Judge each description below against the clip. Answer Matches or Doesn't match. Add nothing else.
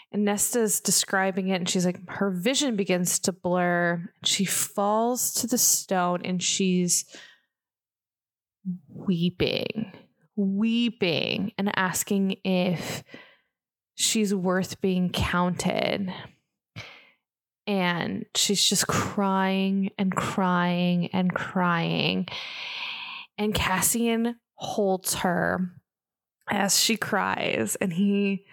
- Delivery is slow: Matches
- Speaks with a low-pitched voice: Doesn't match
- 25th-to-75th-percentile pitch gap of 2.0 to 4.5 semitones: Matches